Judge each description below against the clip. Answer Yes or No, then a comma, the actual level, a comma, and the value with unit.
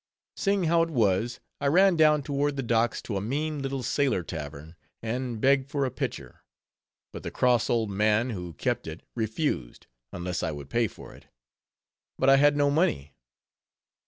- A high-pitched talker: No, low, 125 Hz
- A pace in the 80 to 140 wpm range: No, average, 175 wpm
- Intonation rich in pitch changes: Yes, wide, 6.7 semitones